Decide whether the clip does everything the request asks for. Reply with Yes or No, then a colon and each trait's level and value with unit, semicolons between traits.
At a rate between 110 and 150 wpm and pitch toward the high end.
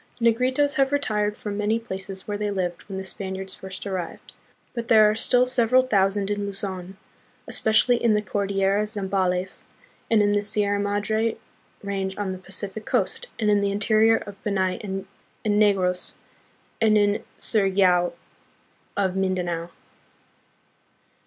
Yes: average, 145 wpm; high, 205 Hz